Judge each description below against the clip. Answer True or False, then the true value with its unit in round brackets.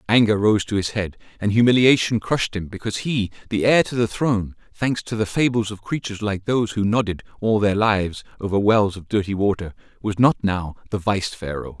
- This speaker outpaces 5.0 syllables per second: True (5.6 syllables/s)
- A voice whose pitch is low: True (105 Hz)